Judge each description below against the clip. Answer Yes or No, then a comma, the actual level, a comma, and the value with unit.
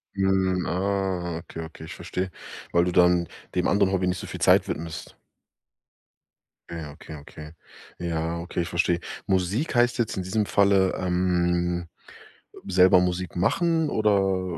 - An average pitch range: No, narrow, 1.8 semitones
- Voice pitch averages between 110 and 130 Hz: No, very low, 90 Hz